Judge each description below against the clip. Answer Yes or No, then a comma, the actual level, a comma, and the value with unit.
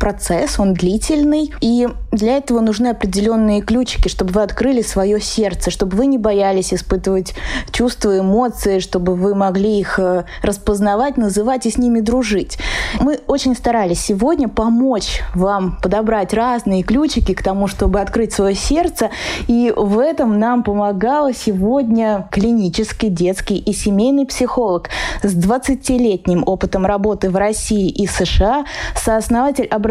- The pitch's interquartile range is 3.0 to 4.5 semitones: Yes, average, 3.7 semitones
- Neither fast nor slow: Yes, average, 135 wpm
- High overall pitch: Yes, high, 215 Hz